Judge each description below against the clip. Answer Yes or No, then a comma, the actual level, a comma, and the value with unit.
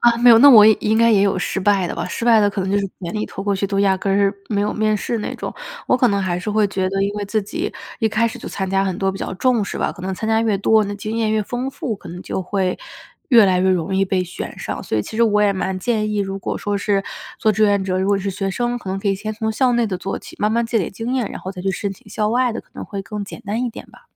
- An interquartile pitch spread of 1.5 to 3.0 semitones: Yes, narrow, 2.4 semitones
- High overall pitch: Yes, high, 205 Hz